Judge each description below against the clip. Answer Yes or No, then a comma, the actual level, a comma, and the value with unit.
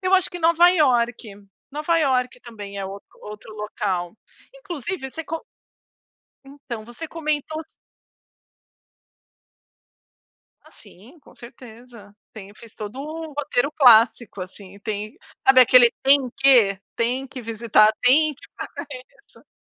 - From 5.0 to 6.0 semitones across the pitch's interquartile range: Yes, average, 5.3 semitones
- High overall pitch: Yes, very high, 250 Hz